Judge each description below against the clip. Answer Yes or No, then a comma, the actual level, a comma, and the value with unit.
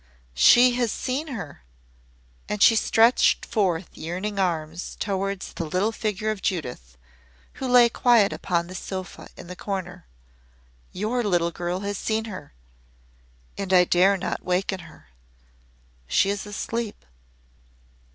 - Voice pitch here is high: Yes, high, 195 Hz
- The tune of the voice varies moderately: Yes, average, 3.6 semitones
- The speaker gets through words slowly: Yes, slow, 130 wpm